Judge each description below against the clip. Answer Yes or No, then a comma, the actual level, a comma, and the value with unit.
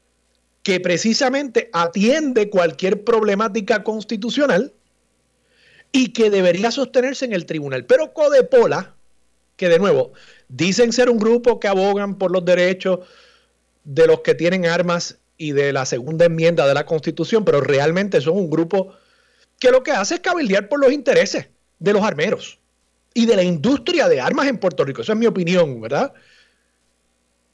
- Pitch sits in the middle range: No, high, 200 Hz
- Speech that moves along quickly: No, average, 155 wpm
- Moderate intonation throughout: No, wide, 7.2 semitones